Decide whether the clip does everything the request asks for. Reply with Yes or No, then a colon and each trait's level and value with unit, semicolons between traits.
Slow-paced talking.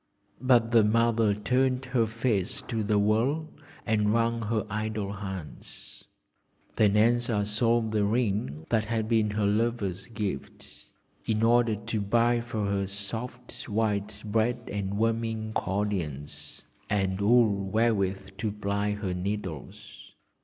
Yes: slow, 130 wpm